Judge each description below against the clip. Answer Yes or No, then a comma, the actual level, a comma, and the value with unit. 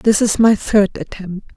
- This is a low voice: No, high, 205 Hz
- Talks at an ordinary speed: Yes, average, 190 wpm